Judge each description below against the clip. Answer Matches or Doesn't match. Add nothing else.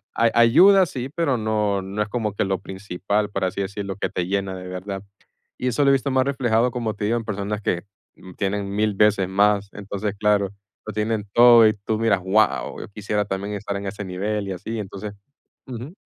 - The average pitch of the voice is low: Matches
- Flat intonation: Matches